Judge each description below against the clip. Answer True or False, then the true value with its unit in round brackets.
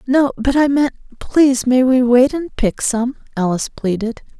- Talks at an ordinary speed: True (165 wpm)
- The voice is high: True (255 Hz)